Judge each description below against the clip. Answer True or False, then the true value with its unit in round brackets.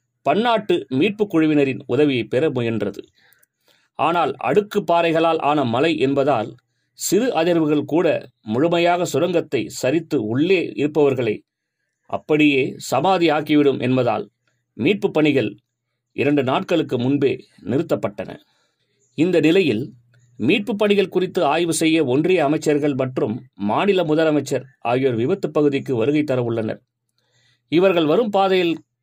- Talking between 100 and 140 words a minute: True (105 wpm)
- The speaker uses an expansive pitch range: False (5.0 semitones)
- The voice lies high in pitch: False (150 Hz)